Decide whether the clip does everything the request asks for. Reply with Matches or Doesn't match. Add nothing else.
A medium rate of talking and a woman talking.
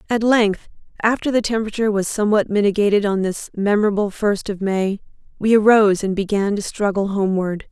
Matches